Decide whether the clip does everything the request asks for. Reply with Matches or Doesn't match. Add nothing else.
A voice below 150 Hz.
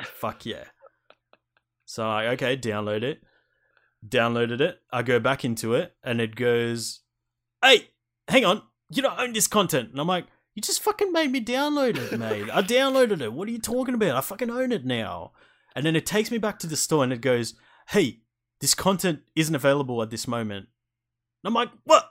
Matches